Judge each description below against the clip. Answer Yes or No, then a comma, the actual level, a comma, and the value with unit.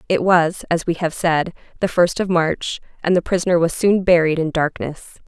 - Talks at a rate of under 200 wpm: No, fast, 205 wpm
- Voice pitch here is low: No, medium, 170 Hz